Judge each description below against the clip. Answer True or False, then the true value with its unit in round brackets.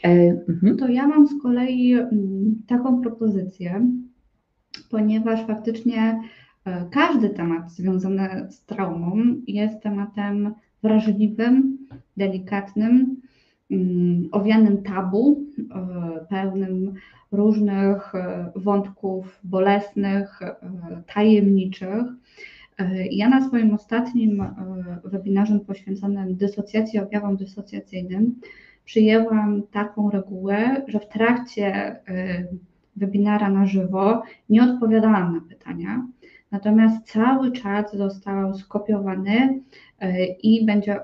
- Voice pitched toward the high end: True (205 Hz)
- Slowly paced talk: True (80 wpm)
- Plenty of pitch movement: False (2.6 semitones)